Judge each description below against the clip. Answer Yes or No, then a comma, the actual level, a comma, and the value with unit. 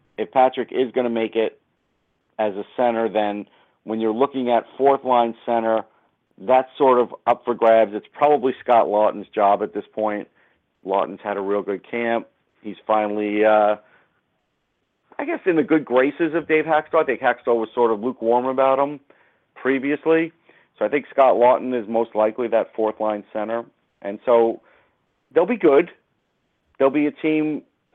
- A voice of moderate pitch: No, low, 115 Hz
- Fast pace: No, average, 175 wpm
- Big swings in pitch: No, average, 3.8 semitones